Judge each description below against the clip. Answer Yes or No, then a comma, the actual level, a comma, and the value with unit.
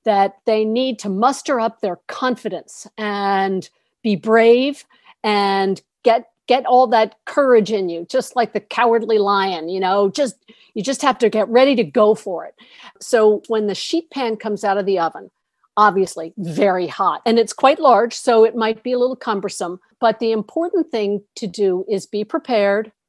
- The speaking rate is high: No, average, 180 wpm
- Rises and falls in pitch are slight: No, average, 3.2 semitones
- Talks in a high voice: Yes, high, 220 Hz